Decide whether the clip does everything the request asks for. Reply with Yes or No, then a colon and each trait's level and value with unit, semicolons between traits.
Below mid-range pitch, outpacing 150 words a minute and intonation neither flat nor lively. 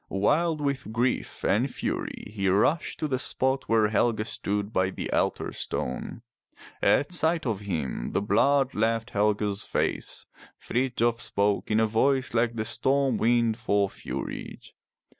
No: low, 115 Hz; average, 145 wpm; average, 4.3 semitones